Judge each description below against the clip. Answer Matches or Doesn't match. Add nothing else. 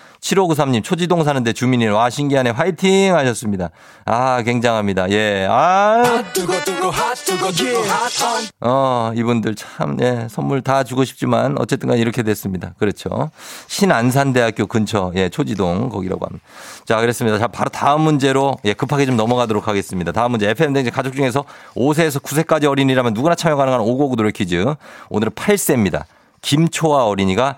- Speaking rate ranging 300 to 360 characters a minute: Matches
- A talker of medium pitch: Doesn't match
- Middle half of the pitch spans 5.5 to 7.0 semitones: Doesn't match